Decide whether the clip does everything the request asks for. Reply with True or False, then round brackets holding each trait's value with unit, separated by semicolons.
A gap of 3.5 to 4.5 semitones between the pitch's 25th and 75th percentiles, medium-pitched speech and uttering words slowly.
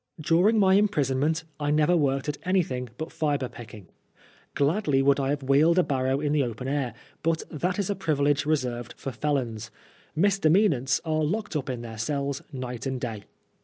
False (3.8 semitones; 145 Hz; 180 wpm)